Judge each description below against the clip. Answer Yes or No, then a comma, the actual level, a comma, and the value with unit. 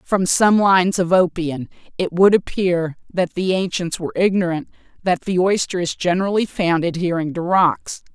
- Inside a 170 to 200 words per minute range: No, average, 160 wpm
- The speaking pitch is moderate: Yes, medium, 180 Hz